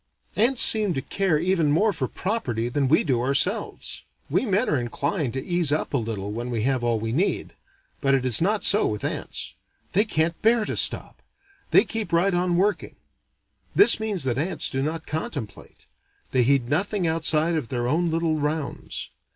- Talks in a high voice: No, medium, 155 Hz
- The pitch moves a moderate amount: No, wide, 6.3 semitones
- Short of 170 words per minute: No, average, 185 wpm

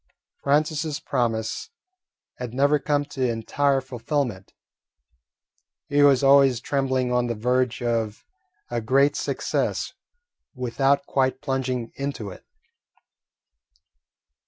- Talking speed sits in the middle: No, slow, 100 wpm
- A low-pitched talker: Yes, low, 130 Hz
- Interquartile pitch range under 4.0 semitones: Yes, average, 2.8 semitones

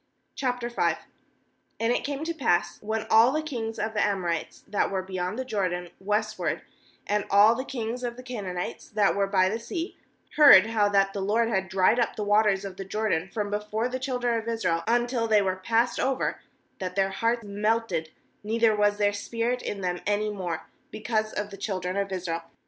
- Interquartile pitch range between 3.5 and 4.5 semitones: No, average, 3.1 semitones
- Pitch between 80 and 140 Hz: No, high, 210 Hz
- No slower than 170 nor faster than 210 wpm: Yes, average, 195 wpm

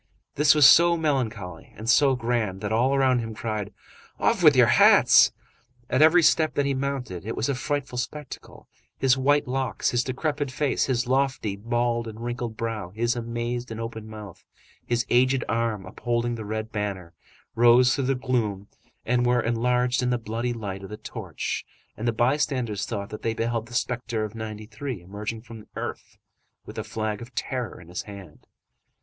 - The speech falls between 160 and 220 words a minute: Yes, average, 180 wpm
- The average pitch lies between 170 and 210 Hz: No, low, 120 Hz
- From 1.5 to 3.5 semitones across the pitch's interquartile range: Yes, average, 2.9 semitones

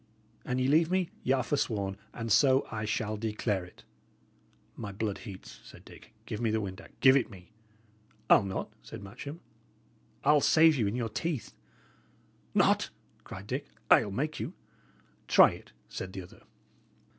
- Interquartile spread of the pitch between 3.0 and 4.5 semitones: No, average, 5.2 semitones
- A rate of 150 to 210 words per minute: Yes, average, 160 wpm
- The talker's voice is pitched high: No, low, 115 Hz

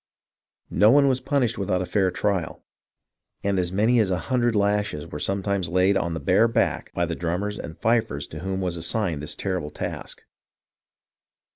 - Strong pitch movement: No, average, 3.7 semitones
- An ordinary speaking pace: Yes, average, 175 wpm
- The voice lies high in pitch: No, very low, 95 Hz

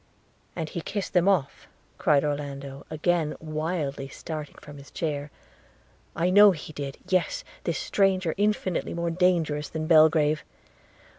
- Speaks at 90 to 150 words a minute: Yes, average, 140 wpm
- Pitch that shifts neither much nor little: Yes, average, 3.4 semitones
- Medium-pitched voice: Yes, medium, 160 Hz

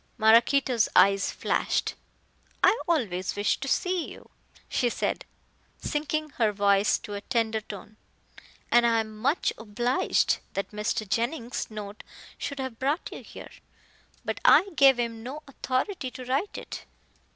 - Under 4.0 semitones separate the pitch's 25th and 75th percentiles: No, average, 4.3 semitones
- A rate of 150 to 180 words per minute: No, average, 140 wpm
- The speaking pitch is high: Yes, high, 235 Hz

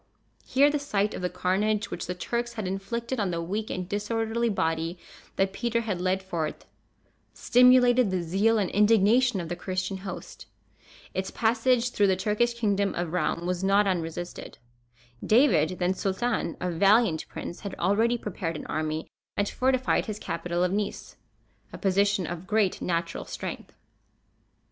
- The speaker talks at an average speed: Yes, average, 160 wpm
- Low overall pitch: No, high, 200 Hz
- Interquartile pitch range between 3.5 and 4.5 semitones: Yes, average, 3.9 semitones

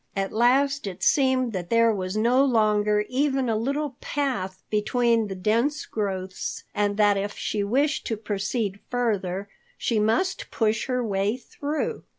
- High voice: Yes, high, 220 Hz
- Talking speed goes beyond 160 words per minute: No, average, 155 wpm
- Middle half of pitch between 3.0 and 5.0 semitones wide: Yes, average, 3.9 semitones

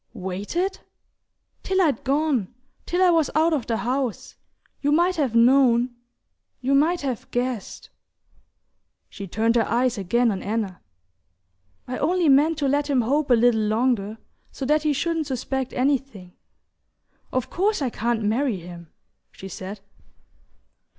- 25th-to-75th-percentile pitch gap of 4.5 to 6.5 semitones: Yes, average, 4.8 semitones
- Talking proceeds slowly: No, average, 145 wpm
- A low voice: No, very high, 255 Hz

